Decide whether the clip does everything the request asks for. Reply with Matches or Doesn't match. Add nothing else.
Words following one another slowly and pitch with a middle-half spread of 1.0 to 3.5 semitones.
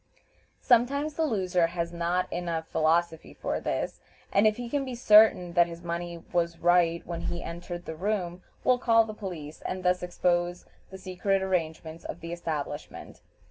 Doesn't match